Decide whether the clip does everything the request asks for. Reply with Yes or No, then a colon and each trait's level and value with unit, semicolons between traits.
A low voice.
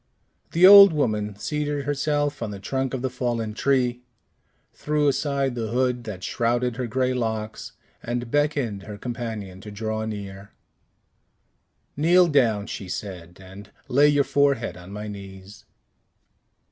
Yes: low, 120 Hz